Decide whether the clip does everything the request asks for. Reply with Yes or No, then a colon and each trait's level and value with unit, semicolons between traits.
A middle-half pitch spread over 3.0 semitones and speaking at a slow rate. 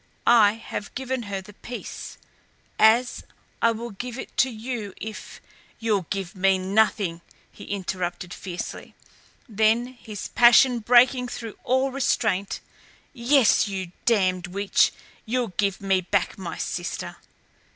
Yes: average, 3.8 semitones; slow, 130 wpm